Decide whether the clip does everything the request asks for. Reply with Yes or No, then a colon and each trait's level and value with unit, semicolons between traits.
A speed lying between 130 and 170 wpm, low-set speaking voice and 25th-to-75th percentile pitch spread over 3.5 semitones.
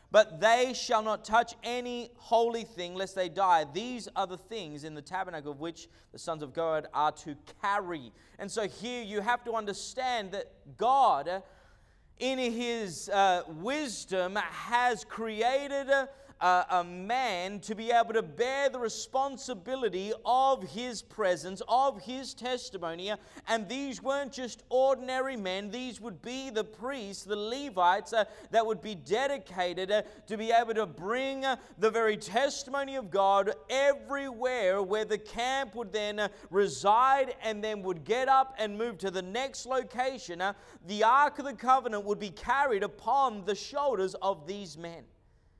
No: average, 160 wpm; high, 220 Hz; average, 4.6 semitones